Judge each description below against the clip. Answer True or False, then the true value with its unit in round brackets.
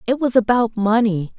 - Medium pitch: False (225 Hz)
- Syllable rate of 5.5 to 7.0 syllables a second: False (4.9 syllables/s)